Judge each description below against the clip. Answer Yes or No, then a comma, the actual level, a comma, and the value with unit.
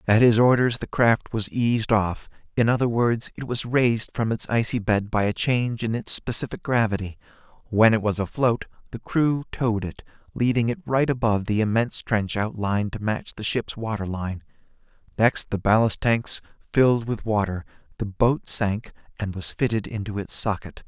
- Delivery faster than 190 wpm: No, average, 180 wpm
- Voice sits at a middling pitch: No, low, 110 Hz